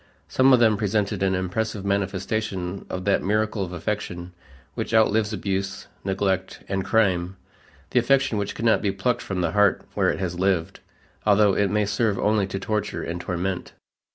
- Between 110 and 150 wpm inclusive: No, average, 170 wpm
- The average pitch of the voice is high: No, low, 100 Hz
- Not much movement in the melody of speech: Yes, narrow, 2.2 semitones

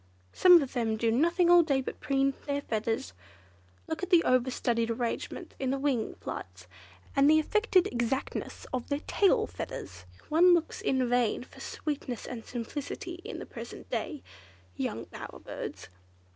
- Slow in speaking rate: No, average, 160 wpm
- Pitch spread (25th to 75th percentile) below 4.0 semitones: No, average, 5.3 semitones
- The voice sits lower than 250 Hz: No, very high, 270 Hz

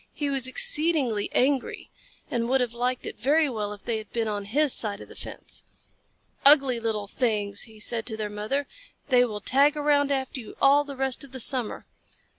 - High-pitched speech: Yes, very high, 250 Hz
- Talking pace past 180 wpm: Yes, average, 200 wpm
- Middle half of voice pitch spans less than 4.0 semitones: No, average, 4.3 semitones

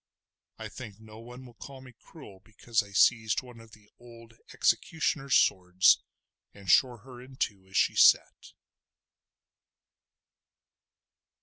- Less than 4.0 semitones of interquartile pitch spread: Yes, average, 3.6 semitones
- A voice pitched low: Yes, low, 115 Hz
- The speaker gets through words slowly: Yes, slow, 130 wpm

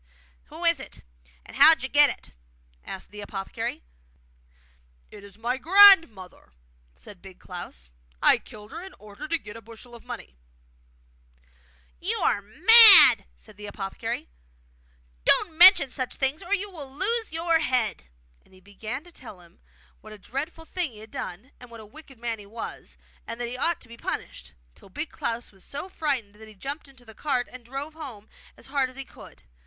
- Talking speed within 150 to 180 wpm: No, average, 190 wpm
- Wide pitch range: Yes, wide, 6.8 semitones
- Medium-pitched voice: No, high, 245 Hz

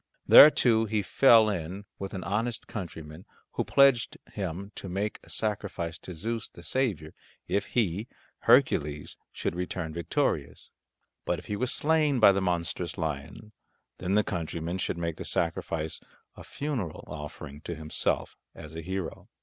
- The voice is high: No, very low, 95 Hz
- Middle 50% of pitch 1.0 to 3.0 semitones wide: No, average, 4.9 semitones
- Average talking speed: Yes, average, 155 wpm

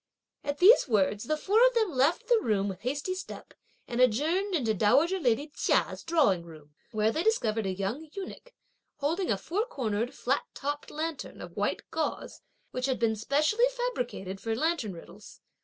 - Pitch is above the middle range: Yes, very high, 275 Hz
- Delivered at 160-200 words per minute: Yes, average, 175 wpm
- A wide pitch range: Yes, wide, 7.9 semitones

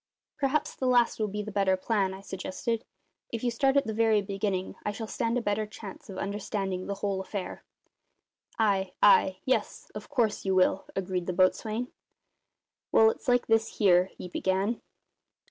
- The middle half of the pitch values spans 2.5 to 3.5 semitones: Yes, average, 3.0 semitones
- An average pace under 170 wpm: No, average, 175 wpm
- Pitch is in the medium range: No, high, 205 Hz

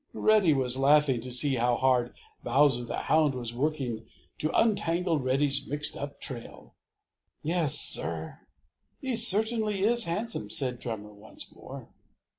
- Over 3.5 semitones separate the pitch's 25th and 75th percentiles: Yes, wide, 5.6 semitones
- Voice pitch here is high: No, medium, 140 Hz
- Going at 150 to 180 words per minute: No, slow, 135 wpm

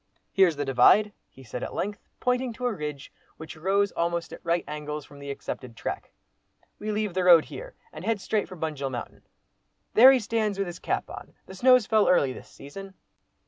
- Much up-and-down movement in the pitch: Yes, wide, 6.1 semitones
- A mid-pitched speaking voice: Yes, medium, 180 Hz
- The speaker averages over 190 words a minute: Yes, average, 200 wpm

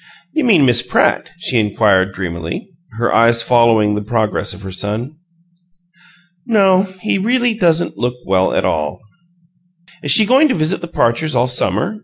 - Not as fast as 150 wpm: No, average, 160 wpm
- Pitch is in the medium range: No, low, 120 Hz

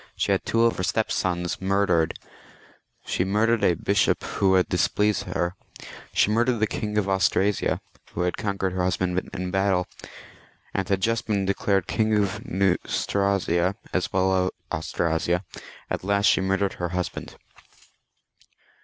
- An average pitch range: No, narrow, 2.1 semitones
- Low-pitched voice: Yes, very low, 95 Hz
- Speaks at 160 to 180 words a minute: No, average, 150 wpm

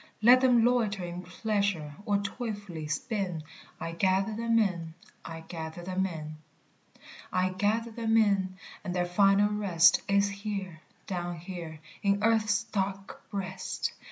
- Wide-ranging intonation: No, average, 3.2 semitones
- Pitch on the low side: No, high, 195 Hz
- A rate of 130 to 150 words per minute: Yes, slow, 135 wpm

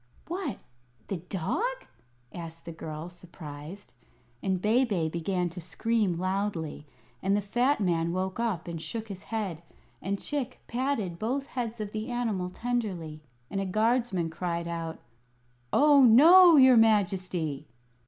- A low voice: No, high, 195 Hz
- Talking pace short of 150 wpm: Yes, slow, 135 wpm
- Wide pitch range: Yes, wide, 5.7 semitones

